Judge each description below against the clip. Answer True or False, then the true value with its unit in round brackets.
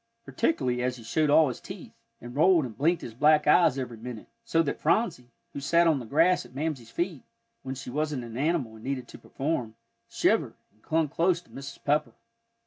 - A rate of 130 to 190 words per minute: False (205 wpm)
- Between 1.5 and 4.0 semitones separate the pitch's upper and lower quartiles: False (4.7 semitones)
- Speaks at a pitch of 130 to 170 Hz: True (140 Hz)